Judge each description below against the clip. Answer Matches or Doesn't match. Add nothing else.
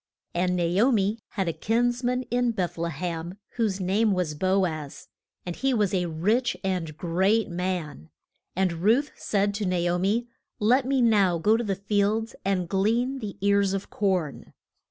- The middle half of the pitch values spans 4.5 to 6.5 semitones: Doesn't match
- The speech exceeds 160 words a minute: Matches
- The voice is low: Doesn't match